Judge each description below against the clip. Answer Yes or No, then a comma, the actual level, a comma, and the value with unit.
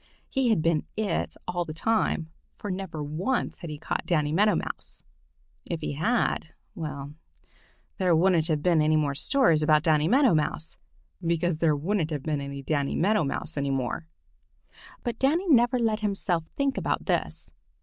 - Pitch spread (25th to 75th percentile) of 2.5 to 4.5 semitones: No, wide, 5.6 semitones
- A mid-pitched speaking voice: Yes, medium, 165 Hz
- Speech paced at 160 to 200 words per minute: Yes, average, 165 wpm